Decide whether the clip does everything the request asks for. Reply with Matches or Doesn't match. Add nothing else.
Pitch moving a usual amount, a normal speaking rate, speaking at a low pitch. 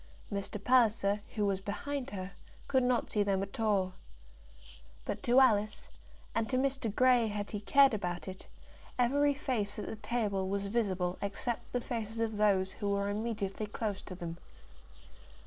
Doesn't match